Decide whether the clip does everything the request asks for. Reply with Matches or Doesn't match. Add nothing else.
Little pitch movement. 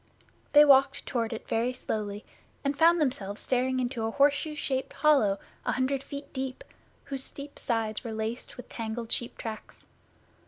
Doesn't match